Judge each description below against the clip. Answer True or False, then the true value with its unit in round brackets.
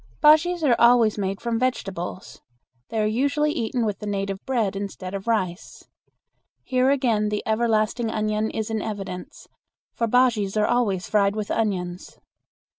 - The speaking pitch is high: True (215 Hz)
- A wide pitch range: False (3.3 semitones)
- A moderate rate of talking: True (150 wpm)